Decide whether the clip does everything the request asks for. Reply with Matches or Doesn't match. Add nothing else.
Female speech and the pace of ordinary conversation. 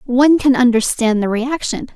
Matches